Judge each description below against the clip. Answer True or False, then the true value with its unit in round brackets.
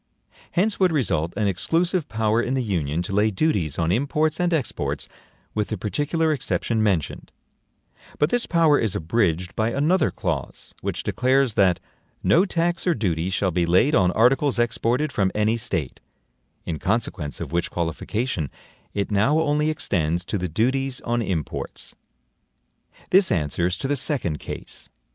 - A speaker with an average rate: True (155 wpm)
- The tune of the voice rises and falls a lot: True (8.5 semitones)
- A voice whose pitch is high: False (110 Hz)